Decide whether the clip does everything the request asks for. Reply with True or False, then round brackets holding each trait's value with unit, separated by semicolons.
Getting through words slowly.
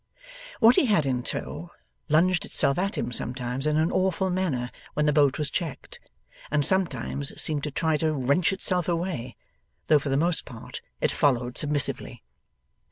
False (165 wpm)